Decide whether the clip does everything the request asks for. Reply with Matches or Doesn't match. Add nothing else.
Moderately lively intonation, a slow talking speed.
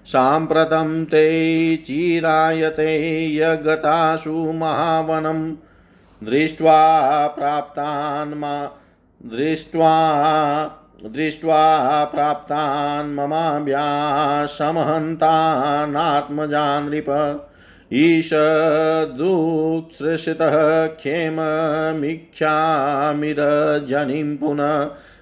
Doesn't match